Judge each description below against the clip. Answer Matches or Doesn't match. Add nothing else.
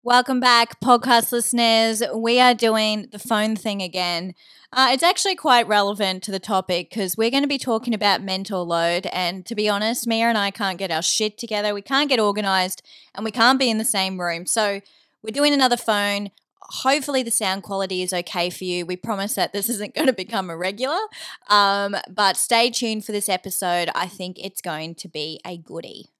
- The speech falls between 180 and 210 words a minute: Matches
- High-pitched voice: Matches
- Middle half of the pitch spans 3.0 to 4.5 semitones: Matches